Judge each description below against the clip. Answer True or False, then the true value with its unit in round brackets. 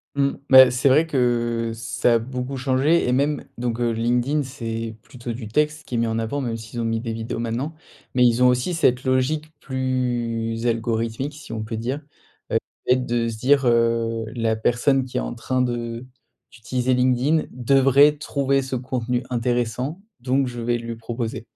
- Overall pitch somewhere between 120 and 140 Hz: True (125 Hz)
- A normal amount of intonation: False (2.3 semitones)